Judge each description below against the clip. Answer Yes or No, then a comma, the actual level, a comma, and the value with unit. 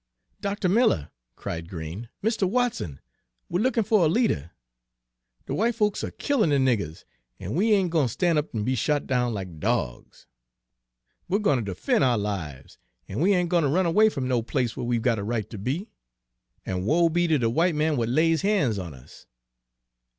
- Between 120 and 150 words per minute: No, average, 200 wpm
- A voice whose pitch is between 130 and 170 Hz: Yes, medium, 140 Hz